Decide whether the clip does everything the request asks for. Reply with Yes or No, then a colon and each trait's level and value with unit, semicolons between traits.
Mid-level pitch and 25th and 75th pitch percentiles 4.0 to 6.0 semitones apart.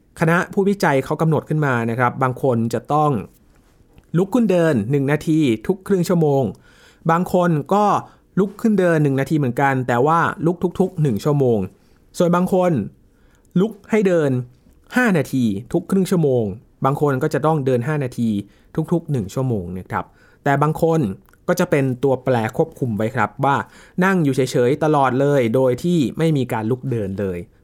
Yes: medium, 145 Hz; average, 5.3 semitones